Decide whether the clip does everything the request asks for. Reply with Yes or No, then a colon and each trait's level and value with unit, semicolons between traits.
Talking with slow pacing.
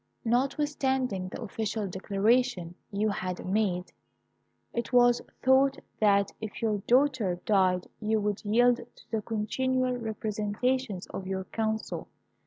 Yes: slow, 120 wpm